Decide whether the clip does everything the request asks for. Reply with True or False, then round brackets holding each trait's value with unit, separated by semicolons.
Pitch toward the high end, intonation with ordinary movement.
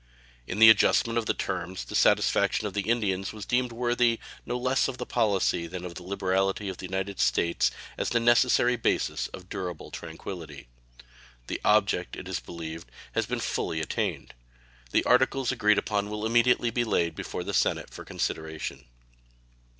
False (100 Hz; 4.8 semitones)